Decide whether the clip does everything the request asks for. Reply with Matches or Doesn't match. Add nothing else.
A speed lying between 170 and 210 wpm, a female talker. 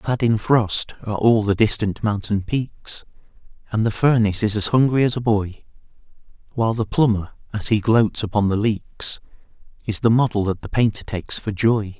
Doesn't match